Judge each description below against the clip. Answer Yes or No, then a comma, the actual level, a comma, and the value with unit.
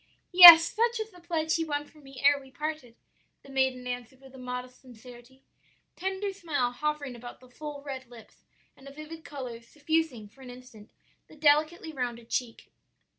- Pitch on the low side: No, very high, 275 Hz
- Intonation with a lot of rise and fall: No, average, 4.0 semitones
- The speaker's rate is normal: Yes, average, 175 wpm